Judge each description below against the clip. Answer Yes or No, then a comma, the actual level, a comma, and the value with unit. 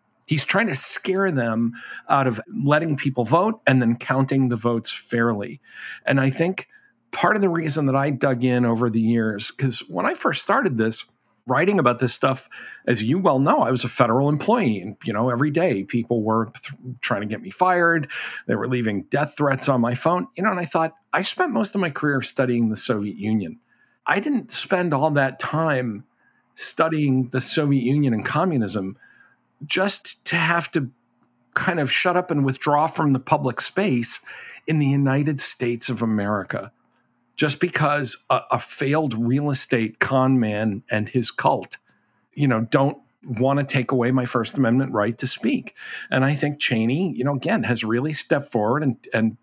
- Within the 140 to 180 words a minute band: No, average, 190 wpm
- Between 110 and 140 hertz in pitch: Yes, low, 135 Hz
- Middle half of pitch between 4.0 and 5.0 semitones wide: Yes, average, 4.5 semitones